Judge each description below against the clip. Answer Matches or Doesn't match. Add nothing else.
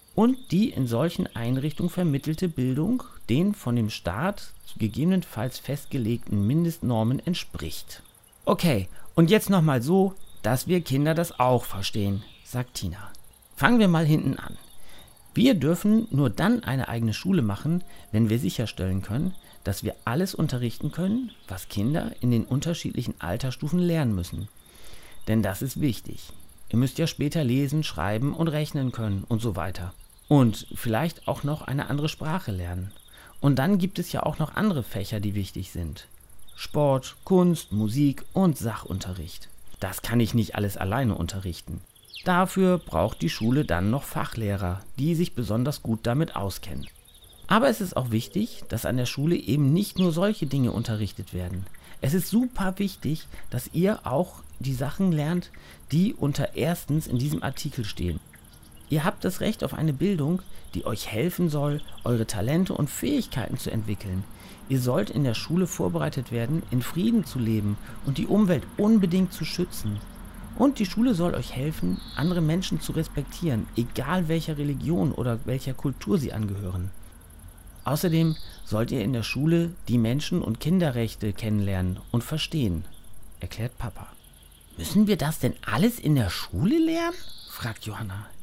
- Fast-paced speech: Doesn't match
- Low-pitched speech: Matches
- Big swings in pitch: Matches